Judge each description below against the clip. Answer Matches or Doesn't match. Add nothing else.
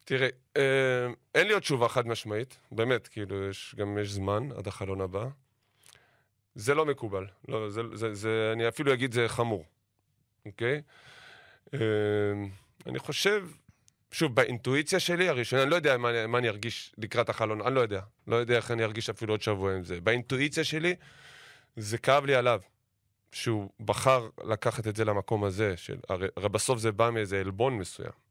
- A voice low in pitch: Matches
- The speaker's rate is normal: Doesn't match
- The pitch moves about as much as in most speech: Matches